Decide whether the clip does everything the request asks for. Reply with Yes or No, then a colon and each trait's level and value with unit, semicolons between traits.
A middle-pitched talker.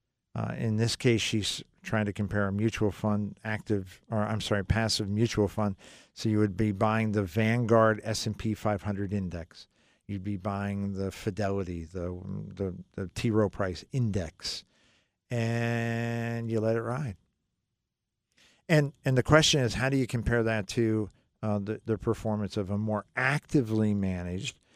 No: low, 110 Hz